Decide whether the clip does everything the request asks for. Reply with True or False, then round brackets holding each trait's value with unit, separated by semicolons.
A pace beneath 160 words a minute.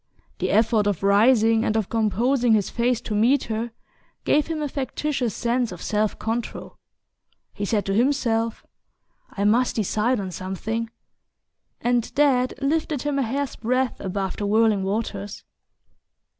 True (150 wpm)